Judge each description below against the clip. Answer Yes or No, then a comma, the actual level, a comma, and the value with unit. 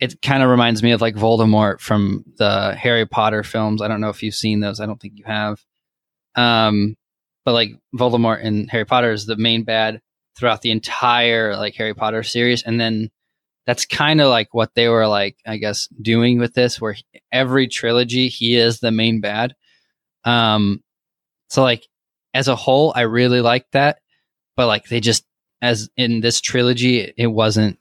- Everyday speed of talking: Yes, average, 190 wpm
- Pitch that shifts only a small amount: Yes, narrow, 2.0 semitones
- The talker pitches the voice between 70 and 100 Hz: No, low, 115 Hz